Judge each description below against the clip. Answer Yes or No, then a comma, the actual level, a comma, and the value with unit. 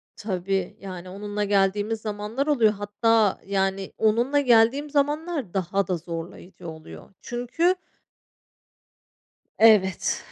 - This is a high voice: Yes, high, 205 Hz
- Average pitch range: Yes, average, 3.8 semitones